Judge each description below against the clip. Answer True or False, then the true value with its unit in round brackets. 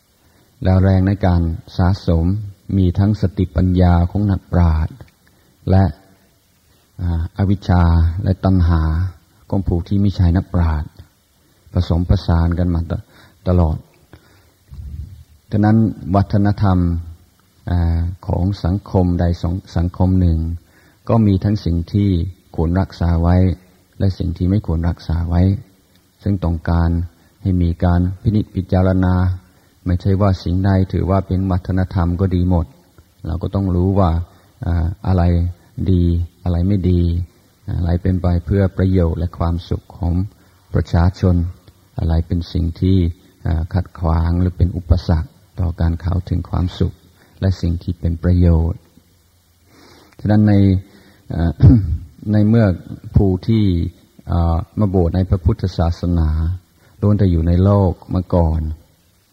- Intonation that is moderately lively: False (2.1 semitones)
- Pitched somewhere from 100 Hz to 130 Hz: False (90 Hz)